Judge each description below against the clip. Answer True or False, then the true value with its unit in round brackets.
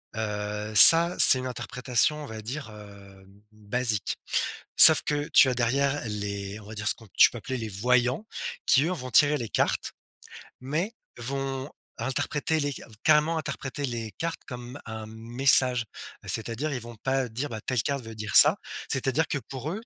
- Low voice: True (125 Hz)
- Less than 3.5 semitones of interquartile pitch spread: False (4.2 semitones)